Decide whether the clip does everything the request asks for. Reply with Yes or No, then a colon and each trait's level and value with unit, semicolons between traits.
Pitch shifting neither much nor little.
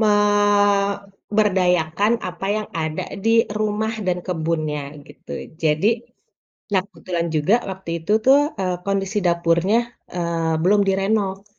Yes: average, 3.6 semitones